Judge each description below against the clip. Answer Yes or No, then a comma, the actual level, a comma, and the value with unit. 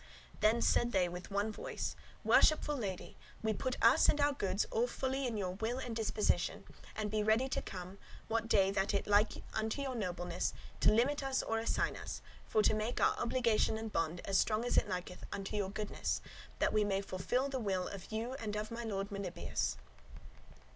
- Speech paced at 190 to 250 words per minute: Yes, average, 195 wpm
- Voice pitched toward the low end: No, high, 215 Hz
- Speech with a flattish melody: No, average, 3.3 semitones